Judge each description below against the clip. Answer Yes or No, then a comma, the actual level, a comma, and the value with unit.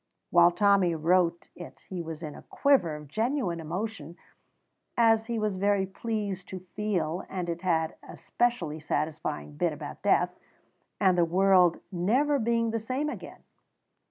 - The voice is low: No, medium, 185 Hz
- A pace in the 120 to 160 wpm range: Yes, average, 155 wpm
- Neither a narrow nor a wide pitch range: Yes, average, 4.7 semitones